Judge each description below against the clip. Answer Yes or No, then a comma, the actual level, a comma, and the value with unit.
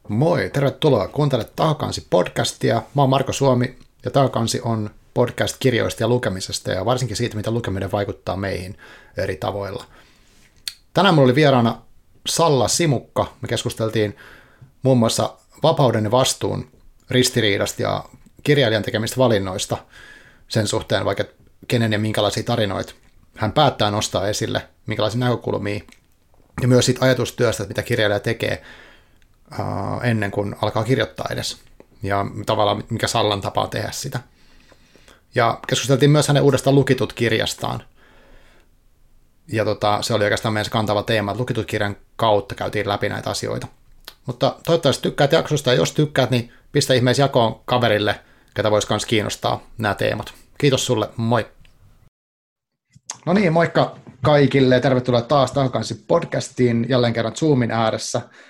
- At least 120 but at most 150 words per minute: Yes, average, 130 wpm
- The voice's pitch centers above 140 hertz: No, low, 120 Hz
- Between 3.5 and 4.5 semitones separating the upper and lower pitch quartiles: Yes, average, 3.8 semitones